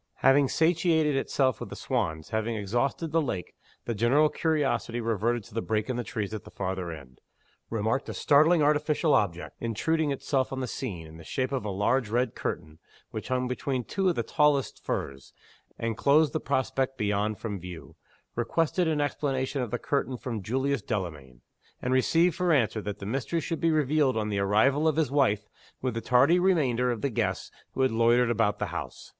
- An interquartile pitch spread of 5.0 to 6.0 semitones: Yes, wide, 5.4 semitones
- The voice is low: Yes, low, 125 Hz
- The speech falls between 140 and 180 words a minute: No, average, 195 wpm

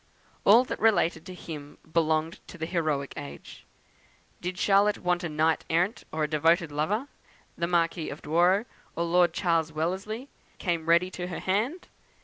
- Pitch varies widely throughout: No, average, 2.8 semitones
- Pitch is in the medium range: Yes, medium, 170 Hz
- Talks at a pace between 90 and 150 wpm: No, average, 160 wpm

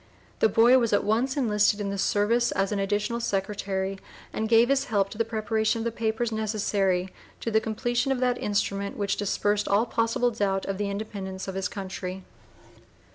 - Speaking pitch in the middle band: No, high, 210 Hz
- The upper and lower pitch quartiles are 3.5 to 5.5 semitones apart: No, narrow, 2.6 semitones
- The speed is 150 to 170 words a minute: No, average, 185 wpm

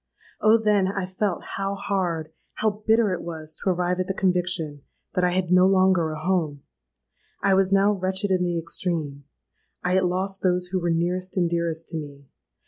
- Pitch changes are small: Yes, narrow, 2.3 semitones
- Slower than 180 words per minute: No, average, 190 wpm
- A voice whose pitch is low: No, medium, 180 Hz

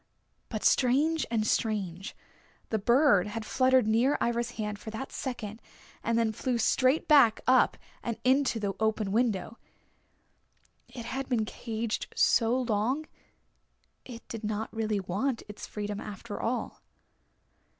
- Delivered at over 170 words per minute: No, slow, 135 wpm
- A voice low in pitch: No, high, 230 Hz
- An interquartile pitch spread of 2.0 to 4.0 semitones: Yes, average, 3.0 semitones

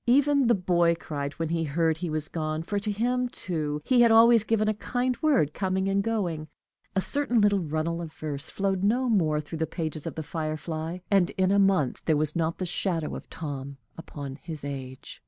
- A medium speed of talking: No, fast, 210 wpm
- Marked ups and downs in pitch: No, average, 4.9 semitones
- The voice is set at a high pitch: No, medium, 170 Hz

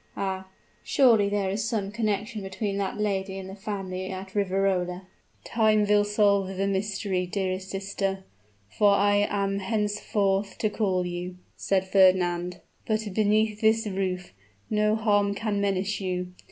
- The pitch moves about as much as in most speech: No, narrow, 1.7 semitones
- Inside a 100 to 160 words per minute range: Yes, average, 145 wpm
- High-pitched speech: Yes, high, 200 Hz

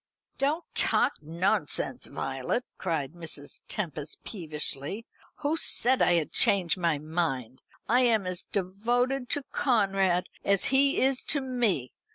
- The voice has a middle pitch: No, high, 195 Hz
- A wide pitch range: Yes, wide, 7.3 semitones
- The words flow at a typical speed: No, slow, 130 wpm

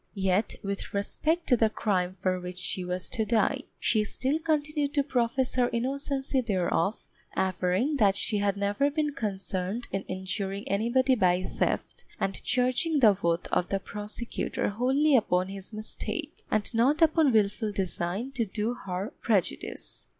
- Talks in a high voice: Yes, high, 215 Hz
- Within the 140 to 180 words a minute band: Yes, average, 155 wpm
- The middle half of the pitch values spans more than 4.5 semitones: Yes, average, 5.2 semitones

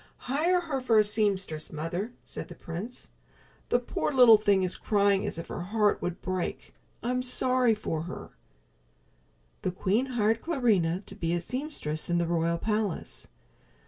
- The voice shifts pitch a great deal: Yes, wide, 6.0 semitones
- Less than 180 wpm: Yes, average, 160 wpm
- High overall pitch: Yes, high, 205 Hz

